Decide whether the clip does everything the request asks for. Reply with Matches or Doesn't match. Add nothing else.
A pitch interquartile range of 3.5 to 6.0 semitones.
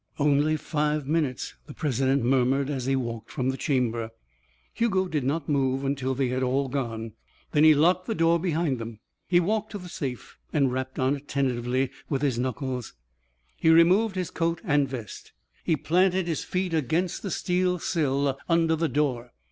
Matches